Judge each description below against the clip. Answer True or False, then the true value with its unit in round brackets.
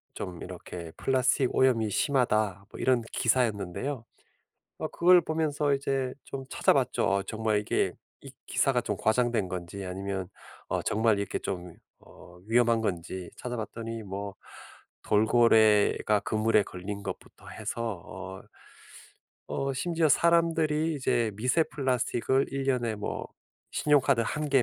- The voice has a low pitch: True (115 Hz)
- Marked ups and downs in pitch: False (5.0 semitones)